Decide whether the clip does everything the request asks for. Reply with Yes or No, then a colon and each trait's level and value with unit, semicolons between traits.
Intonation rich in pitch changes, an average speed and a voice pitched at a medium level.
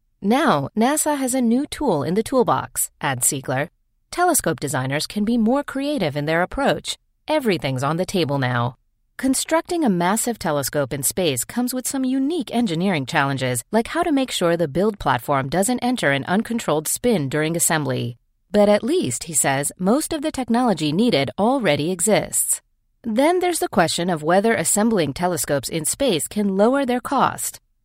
No: wide, 8.9 semitones; average, 170 wpm; high, 205 Hz